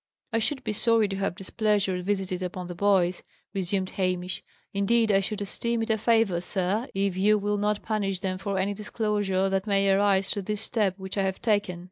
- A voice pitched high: Yes, high, 200 Hz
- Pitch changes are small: Yes, narrow, 2.0 semitones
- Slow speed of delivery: No, average, 200 wpm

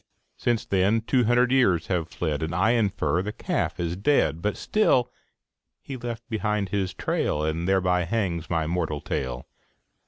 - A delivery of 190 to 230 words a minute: No, average, 160 wpm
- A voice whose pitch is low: Yes, very low, 95 Hz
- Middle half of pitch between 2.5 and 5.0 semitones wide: No, wide, 5.4 semitones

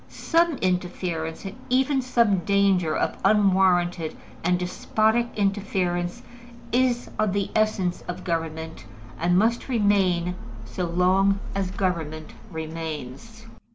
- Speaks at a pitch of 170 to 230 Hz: Yes, medium, 185 Hz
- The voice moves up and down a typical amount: Yes, average, 3.4 semitones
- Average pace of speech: No, slow, 110 wpm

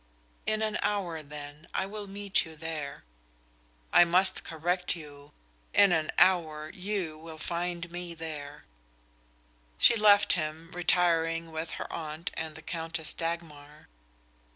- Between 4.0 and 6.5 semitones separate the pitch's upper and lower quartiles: No, narrow, 2.4 semitones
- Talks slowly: Yes, slow, 130 wpm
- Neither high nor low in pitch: Yes, medium, 165 Hz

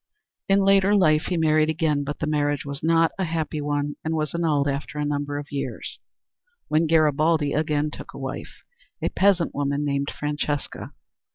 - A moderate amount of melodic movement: No, narrow, 1.9 semitones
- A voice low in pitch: No, medium, 150 Hz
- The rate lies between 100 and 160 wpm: No, average, 175 wpm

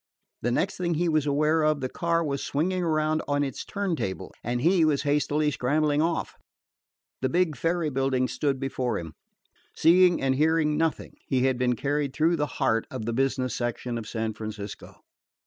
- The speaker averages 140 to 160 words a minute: No, average, 180 wpm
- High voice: No, medium, 145 Hz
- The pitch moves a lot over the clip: No, average, 3.9 semitones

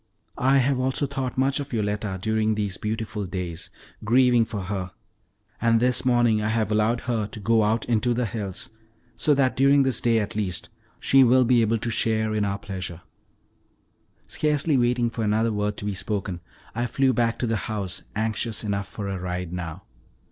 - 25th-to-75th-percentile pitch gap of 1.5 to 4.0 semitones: Yes, average, 3.1 semitones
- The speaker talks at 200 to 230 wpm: No, average, 185 wpm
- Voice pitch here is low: Yes, low, 110 Hz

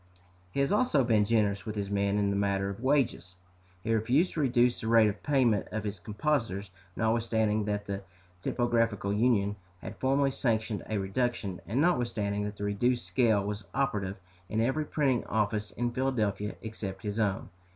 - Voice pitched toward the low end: Yes, low, 110 Hz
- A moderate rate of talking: Yes, average, 170 wpm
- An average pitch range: Yes, average, 3.2 semitones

